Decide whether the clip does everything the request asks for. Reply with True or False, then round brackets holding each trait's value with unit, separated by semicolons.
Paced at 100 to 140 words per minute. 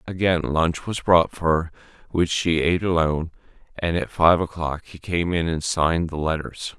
False (185 wpm)